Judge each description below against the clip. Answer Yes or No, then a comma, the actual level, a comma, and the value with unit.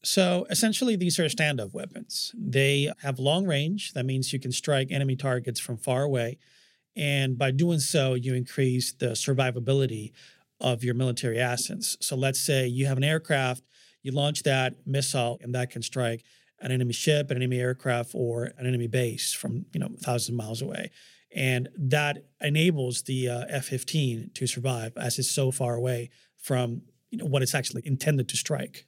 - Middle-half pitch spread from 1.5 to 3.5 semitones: Yes, average, 2.7 semitones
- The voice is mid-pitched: No, low, 130 Hz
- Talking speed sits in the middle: Yes, average, 180 wpm